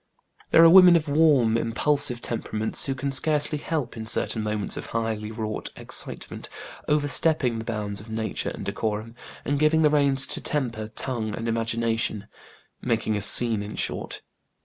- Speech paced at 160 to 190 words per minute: Yes, average, 165 wpm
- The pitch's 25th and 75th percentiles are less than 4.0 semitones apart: No, average, 4.8 semitones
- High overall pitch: No, low, 115 Hz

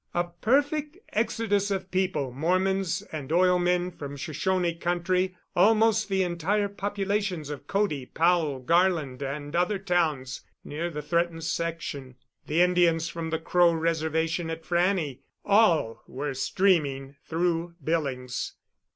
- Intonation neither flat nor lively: Yes, average, 3.4 semitones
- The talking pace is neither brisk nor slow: No, slow, 125 wpm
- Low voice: No, medium, 170 Hz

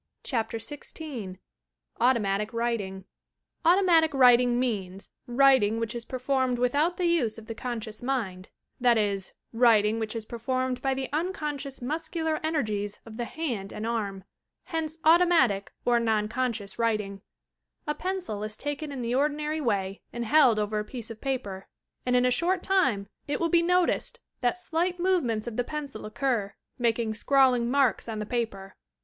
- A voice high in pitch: Yes, high, 245 Hz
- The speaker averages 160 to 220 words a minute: Yes, average, 165 wpm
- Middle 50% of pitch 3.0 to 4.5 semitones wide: No, average, 5.2 semitones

